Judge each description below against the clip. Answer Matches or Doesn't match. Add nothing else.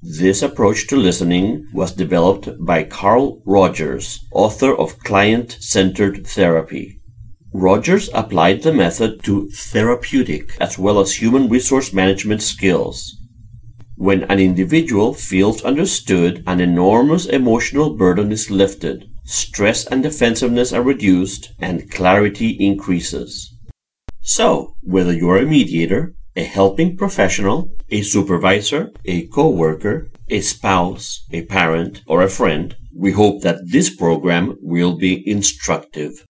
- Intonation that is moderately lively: Matches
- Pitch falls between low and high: Doesn't match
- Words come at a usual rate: Doesn't match